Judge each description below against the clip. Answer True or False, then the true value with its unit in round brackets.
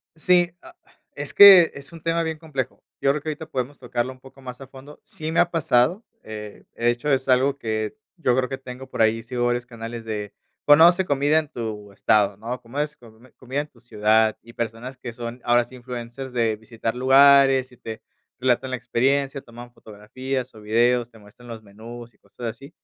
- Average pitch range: True (3.3 semitones)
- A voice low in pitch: True (125 Hz)